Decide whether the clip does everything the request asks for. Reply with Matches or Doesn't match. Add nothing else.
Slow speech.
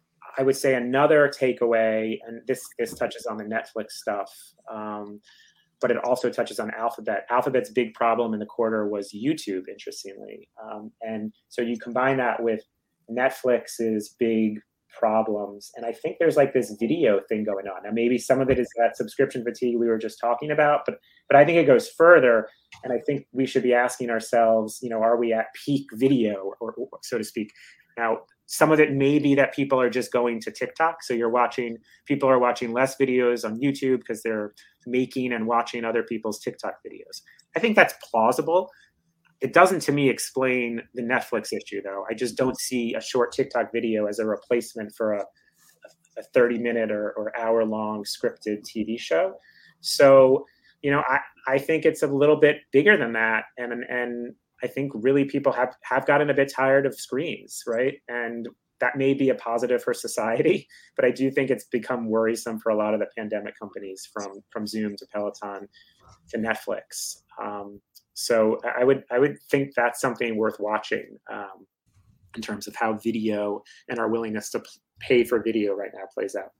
Doesn't match